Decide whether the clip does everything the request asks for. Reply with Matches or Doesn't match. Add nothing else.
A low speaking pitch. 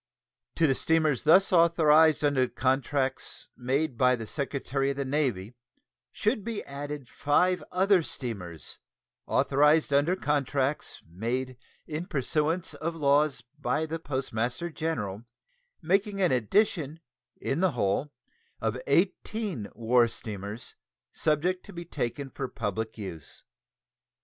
Doesn't match